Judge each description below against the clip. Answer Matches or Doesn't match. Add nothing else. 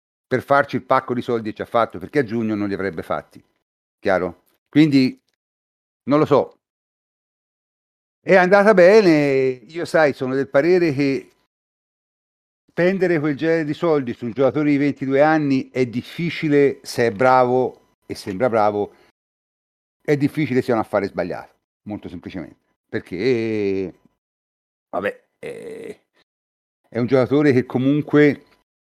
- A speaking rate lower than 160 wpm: Matches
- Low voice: Matches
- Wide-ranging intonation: Matches